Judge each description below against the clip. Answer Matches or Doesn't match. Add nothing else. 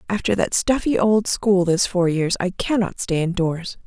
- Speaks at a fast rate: Doesn't match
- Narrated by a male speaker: Doesn't match